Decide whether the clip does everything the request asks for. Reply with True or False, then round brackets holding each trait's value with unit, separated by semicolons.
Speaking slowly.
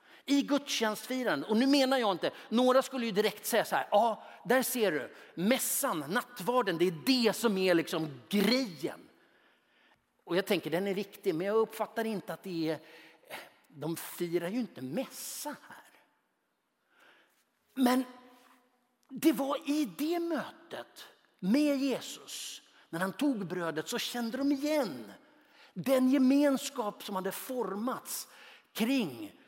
False (140 wpm)